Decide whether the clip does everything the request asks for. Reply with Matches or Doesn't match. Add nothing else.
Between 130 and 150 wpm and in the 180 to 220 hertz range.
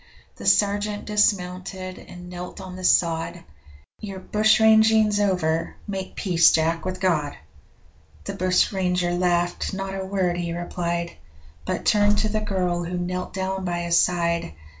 Matches